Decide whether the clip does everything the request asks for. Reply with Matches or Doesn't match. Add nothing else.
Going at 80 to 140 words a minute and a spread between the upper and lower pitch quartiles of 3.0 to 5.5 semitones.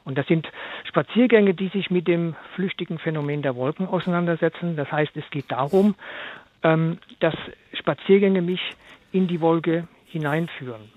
Matches